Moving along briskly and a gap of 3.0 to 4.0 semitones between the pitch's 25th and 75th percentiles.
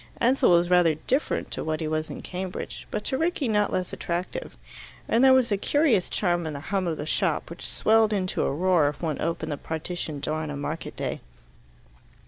No: fast, 210 wpm; average, 4.9 semitones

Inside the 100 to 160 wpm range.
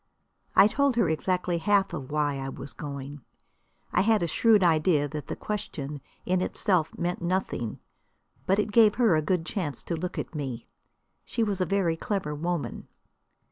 No: average, 175 wpm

